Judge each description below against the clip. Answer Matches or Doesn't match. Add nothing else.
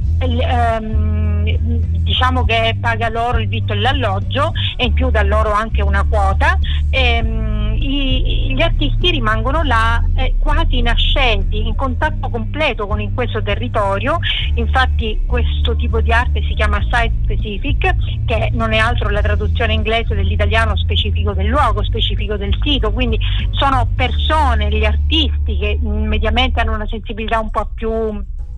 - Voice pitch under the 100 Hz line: Matches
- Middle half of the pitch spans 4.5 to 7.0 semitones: Matches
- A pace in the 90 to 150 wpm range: Matches